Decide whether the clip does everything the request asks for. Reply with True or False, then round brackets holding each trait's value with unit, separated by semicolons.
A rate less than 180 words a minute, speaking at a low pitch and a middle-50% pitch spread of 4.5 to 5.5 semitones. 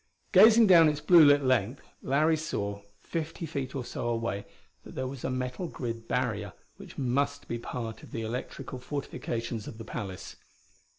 False (170 wpm; 130 Hz; 4.1 semitones)